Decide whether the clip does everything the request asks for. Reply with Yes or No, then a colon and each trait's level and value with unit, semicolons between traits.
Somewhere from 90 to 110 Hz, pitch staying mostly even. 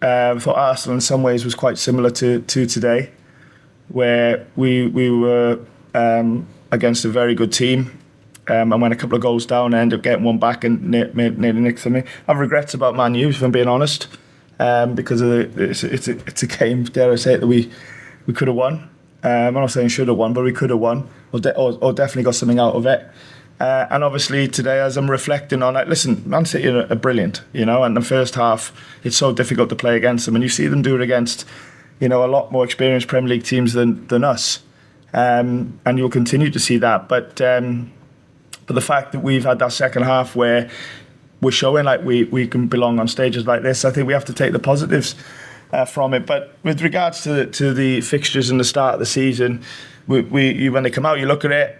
No: low, 125 Hz; narrow, 2.0 semitones